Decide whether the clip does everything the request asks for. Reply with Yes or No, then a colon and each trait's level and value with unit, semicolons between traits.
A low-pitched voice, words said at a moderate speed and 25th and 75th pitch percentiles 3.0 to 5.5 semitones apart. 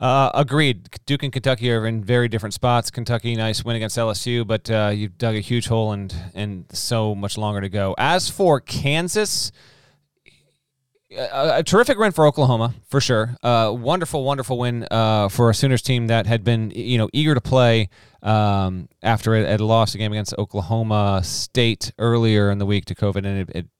Yes: low, 115 Hz; average, 190 wpm; average, 3.3 semitones